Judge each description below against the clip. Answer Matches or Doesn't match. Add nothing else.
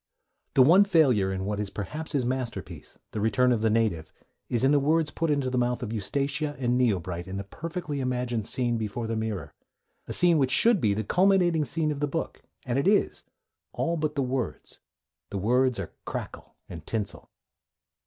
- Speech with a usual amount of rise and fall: Doesn't match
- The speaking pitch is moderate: Doesn't match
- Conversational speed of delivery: Matches